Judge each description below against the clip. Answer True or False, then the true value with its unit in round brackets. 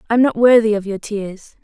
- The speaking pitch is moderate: False (220 Hz)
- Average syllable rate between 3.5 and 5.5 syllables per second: False (6.0 syllables/s)